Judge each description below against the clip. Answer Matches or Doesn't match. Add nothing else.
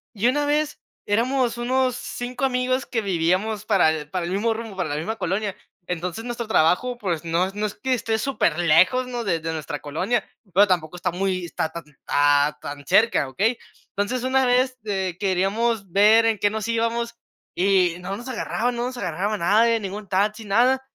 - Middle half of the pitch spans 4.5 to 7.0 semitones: Matches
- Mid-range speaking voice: Doesn't match